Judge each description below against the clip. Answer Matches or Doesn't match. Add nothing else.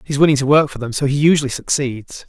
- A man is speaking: Matches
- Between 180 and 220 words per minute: Doesn't match